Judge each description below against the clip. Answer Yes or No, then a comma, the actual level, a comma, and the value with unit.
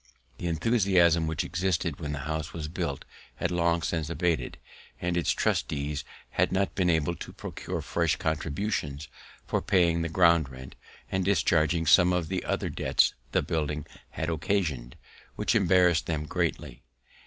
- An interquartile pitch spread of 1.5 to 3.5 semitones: Yes, average, 2.7 semitones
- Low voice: Yes, very low, 85 Hz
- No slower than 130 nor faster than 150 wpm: Yes, average, 145 wpm